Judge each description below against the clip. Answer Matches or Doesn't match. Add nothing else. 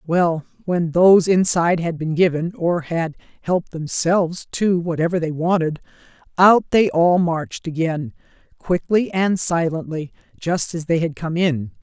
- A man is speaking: Doesn't match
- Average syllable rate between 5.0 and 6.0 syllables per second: Doesn't match